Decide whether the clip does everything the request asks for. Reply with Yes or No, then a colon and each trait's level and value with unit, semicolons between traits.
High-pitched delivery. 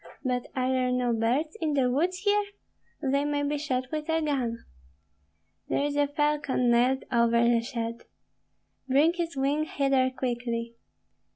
Yes: very high, 265 Hz